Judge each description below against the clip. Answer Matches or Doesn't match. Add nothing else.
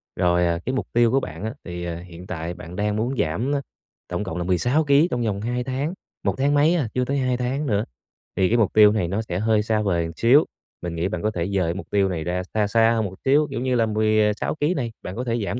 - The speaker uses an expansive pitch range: Matches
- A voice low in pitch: Matches